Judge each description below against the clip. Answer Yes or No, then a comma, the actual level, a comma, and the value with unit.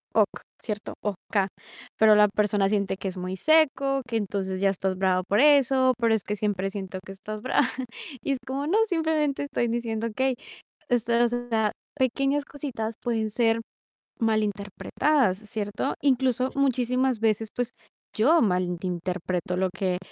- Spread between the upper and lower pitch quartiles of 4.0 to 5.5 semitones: Yes, average, 4.8 semitones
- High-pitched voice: Yes, high, 225 Hz